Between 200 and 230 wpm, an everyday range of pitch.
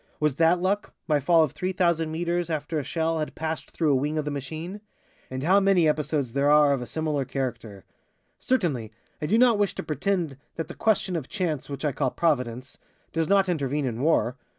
Yes: fast, 205 wpm; average, 3.9 semitones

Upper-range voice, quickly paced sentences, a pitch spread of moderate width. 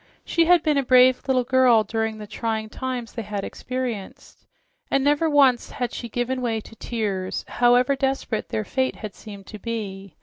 No: high, 240 Hz; average, 180 wpm; average, 3.2 semitones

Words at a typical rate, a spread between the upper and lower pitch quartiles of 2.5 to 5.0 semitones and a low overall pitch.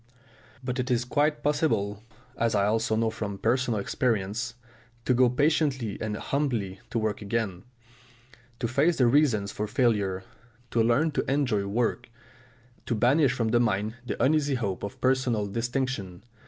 Yes: average, 155 wpm; average, 3.9 semitones; low, 120 Hz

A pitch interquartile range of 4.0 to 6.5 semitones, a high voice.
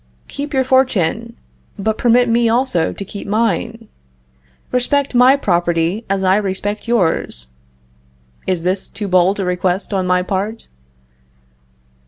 Yes: average, 4.3 semitones; high, 205 Hz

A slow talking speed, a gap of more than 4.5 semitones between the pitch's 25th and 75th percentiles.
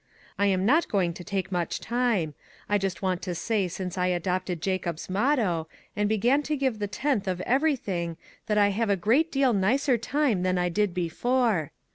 No: average, 195 wpm; average, 5.0 semitones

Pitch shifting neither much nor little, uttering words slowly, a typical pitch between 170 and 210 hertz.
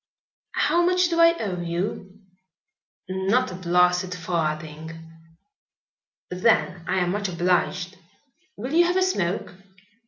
Yes: average, 4.4 semitones; slow, 120 wpm; medium, 185 Hz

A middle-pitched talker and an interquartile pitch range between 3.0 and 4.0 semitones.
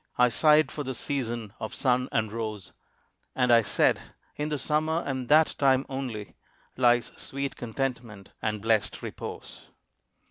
No: low, 125 Hz; average, 3.6 semitones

